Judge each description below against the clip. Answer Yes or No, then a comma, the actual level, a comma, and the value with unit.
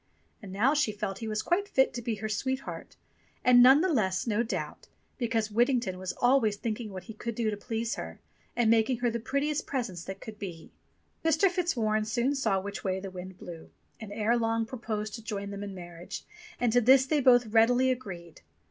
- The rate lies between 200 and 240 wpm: Yes, fast, 205 wpm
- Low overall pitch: No, high, 225 Hz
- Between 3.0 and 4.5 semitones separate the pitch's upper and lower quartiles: Yes, average, 3.6 semitones